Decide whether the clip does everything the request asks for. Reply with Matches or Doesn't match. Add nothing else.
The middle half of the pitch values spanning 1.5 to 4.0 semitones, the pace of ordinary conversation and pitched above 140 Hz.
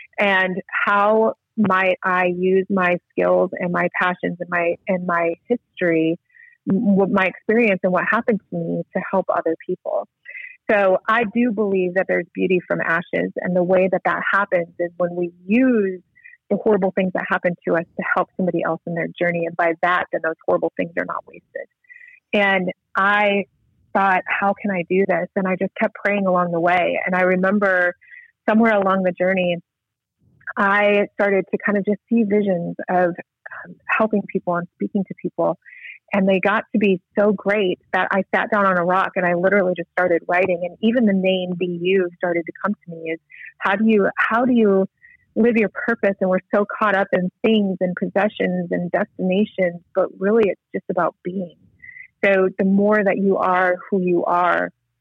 Matches